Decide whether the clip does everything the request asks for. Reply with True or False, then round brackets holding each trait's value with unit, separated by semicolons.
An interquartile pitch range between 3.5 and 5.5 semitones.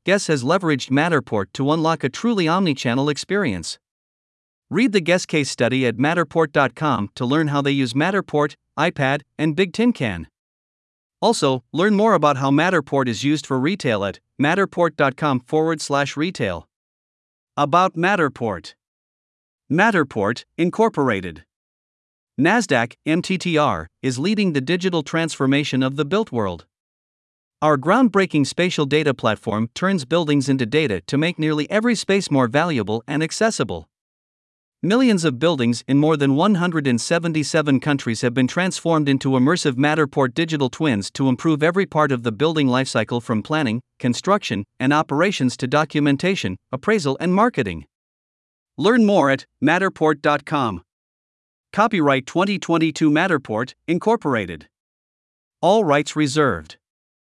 True (4.5 semitones)